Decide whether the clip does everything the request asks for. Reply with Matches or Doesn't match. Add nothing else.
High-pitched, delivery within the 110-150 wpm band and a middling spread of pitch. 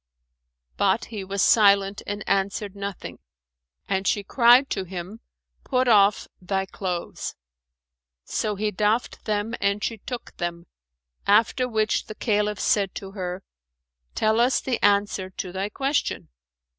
Doesn't match